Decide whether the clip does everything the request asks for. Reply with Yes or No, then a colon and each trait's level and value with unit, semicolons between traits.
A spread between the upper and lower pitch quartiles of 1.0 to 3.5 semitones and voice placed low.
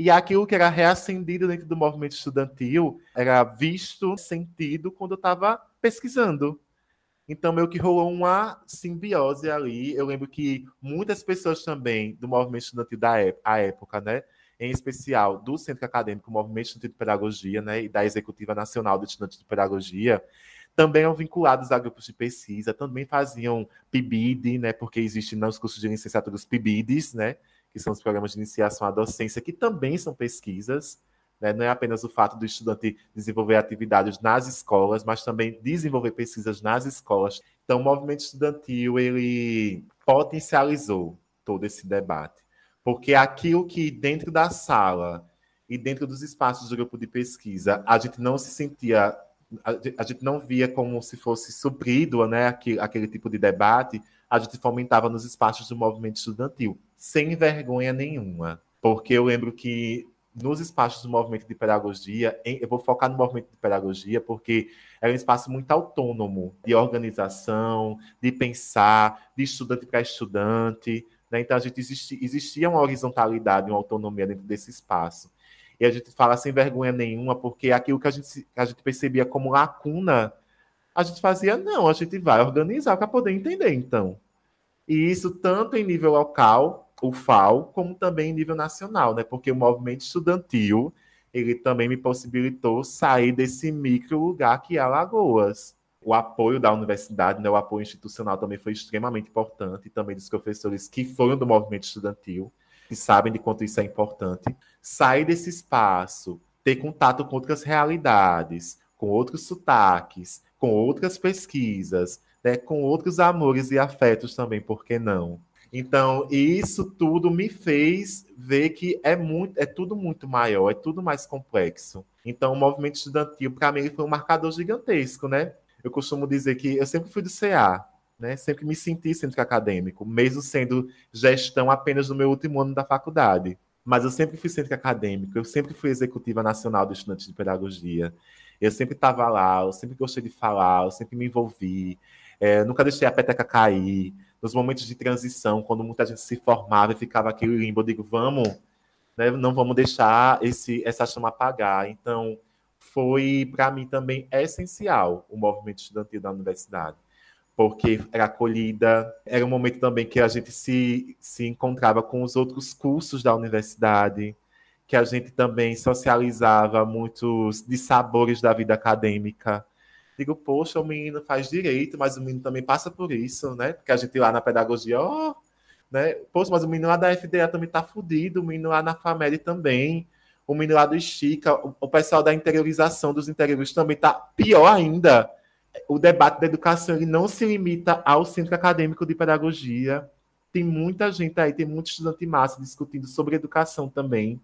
No: average, 5.1 semitones; low, 125 Hz